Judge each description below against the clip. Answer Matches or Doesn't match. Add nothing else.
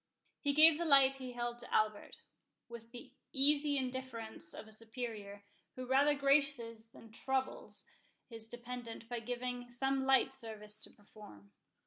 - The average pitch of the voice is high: Matches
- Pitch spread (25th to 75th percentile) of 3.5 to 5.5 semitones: Doesn't match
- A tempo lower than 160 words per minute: Matches